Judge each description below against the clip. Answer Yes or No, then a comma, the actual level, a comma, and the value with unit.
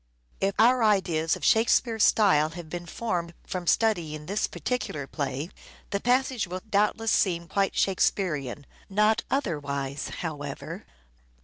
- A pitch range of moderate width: No, wide, 5.8 semitones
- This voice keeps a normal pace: No, slow, 125 wpm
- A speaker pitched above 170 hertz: Yes, medium, 185 Hz